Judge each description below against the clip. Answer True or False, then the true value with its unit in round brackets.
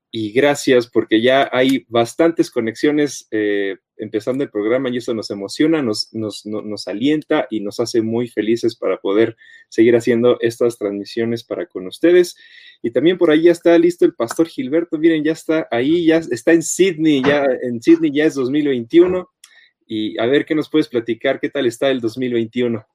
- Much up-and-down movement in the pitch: True (6.2 semitones)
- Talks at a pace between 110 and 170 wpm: False (185 wpm)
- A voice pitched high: False (140 Hz)